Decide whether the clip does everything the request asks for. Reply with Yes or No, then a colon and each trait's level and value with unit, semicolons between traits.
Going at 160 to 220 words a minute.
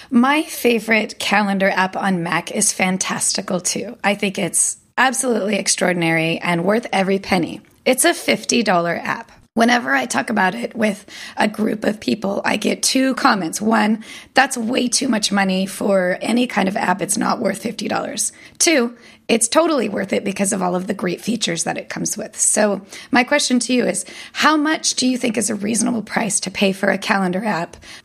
Yes: average, 190 wpm